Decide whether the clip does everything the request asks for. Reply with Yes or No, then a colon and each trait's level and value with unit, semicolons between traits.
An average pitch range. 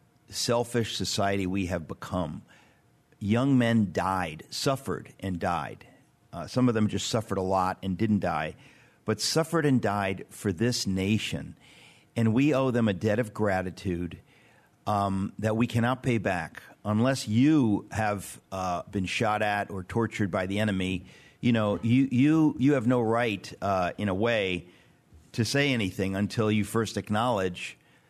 Yes: average, 3.8 semitones